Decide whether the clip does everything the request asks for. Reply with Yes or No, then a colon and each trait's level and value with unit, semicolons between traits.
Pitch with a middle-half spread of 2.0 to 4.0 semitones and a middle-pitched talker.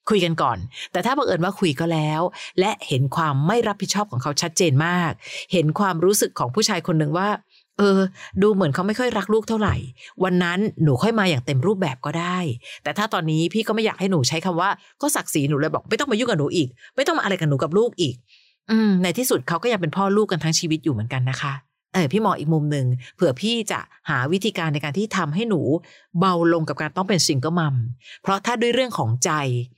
No: average, 5.1 semitones; medium, 175 Hz